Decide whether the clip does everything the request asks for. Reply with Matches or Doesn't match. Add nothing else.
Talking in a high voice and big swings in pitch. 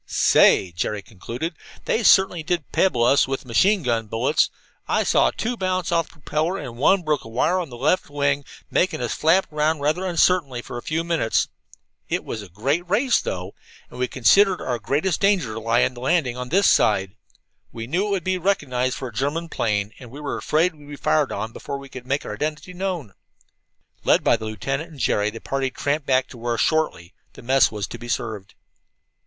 Doesn't match